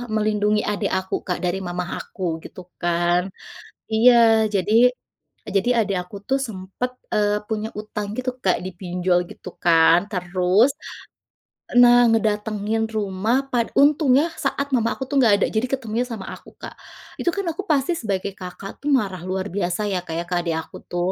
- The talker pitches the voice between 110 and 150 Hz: No, high, 205 Hz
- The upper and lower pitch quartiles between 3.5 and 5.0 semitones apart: Yes, average, 3.8 semitones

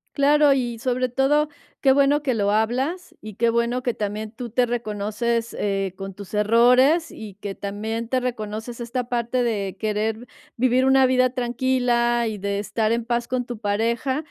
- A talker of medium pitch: No, high, 235 Hz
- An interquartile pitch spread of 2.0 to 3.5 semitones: Yes, average, 2.9 semitones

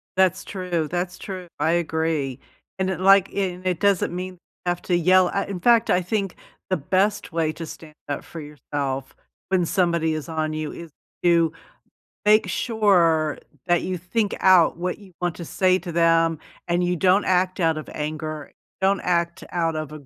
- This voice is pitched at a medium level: Yes, medium, 175 Hz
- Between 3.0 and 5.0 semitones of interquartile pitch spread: No, narrow, 2.5 semitones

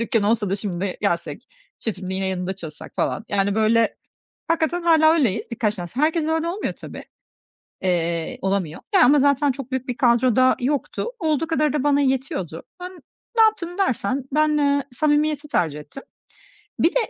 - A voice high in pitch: Yes, very high, 255 Hz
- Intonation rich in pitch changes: Yes, wide, 7.6 semitones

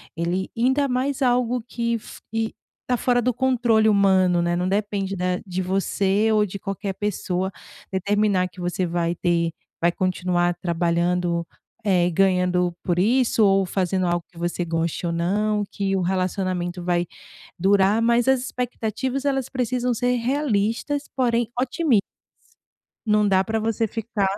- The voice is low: No, high, 195 Hz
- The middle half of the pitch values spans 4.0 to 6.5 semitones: Yes, average, 4.6 semitones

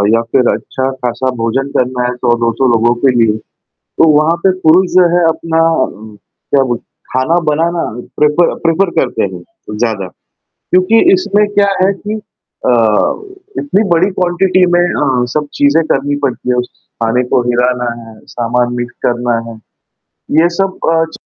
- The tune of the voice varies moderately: No, wide, 6.2 semitones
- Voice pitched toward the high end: No, low, 135 Hz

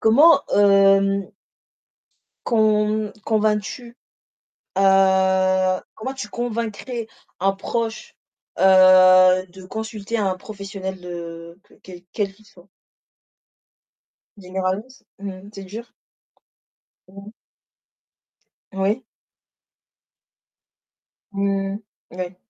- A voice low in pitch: No, high, 195 Hz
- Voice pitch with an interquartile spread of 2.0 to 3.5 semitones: Yes, narrow, 2.5 semitones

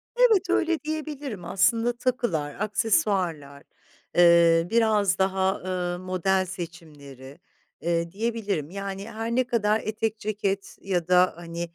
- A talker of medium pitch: No, high, 195 Hz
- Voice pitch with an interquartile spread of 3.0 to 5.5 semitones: Yes, average, 4.6 semitones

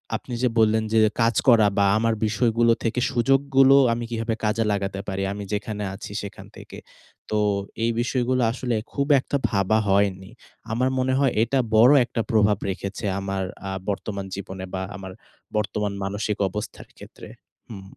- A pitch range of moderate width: Yes, average, 3.2 semitones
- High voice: No, low, 110 Hz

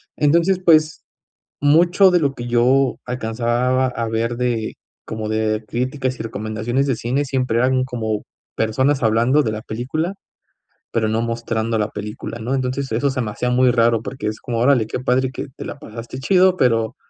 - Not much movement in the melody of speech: No, average, 3.1 semitones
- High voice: No, low, 125 Hz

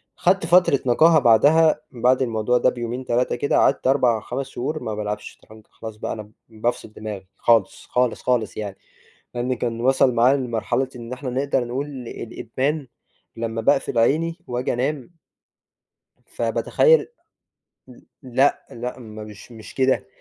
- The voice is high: No, low, 125 Hz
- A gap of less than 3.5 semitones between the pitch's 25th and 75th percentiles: Yes, average, 2.9 semitones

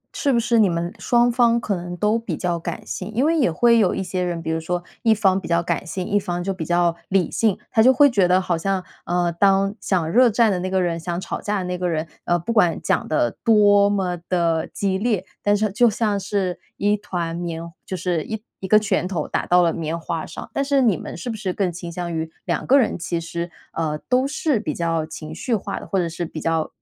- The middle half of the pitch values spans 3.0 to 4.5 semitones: Yes, average, 3.8 semitones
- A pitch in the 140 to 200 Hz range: Yes, medium, 185 Hz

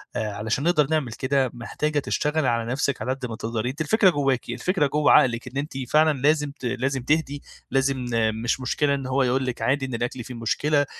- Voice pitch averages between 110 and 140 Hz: Yes, low, 135 Hz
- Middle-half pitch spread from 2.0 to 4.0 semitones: Yes, average, 3.1 semitones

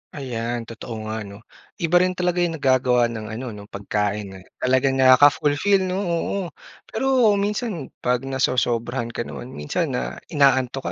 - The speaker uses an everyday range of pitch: No, wide, 6.6 semitones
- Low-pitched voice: Yes, low, 130 Hz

